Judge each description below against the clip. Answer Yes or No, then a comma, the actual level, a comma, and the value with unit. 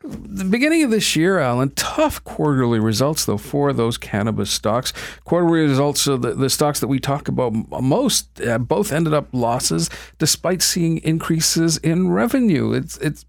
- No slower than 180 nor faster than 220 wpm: No, average, 165 wpm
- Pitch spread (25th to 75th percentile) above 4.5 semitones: Yes, average, 5.2 semitones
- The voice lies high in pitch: No, medium, 150 Hz